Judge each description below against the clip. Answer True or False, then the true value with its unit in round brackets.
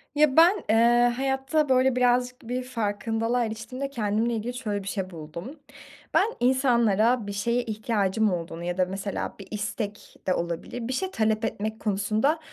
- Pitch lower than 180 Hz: False (225 Hz)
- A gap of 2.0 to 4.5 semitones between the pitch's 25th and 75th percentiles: True (3.6 semitones)